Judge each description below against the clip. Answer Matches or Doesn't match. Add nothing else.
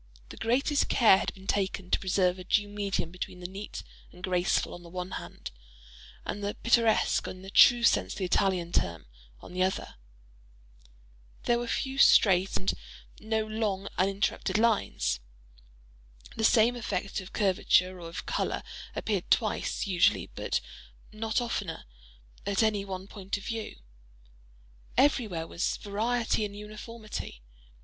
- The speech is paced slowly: Doesn't match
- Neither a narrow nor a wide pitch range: Matches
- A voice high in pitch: Matches